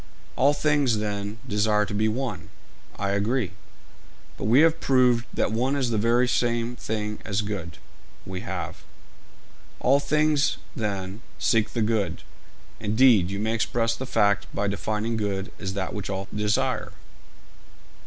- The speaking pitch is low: Yes, low, 110 Hz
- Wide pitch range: No, average, 3.3 semitones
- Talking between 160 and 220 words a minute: No, average, 145 wpm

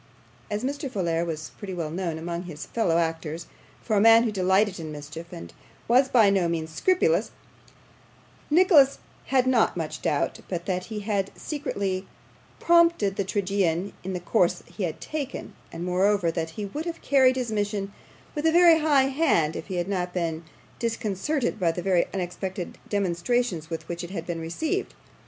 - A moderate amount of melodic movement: No, wide, 6.0 semitones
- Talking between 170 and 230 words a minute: Yes, average, 175 wpm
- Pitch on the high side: Yes, high, 195 Hz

